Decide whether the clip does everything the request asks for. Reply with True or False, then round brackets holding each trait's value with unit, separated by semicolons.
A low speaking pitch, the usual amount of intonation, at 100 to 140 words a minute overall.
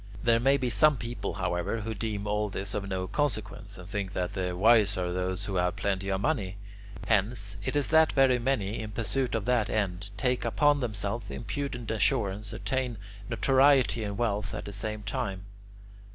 False (105 Hz; 3.7 semitones; 185 wpm)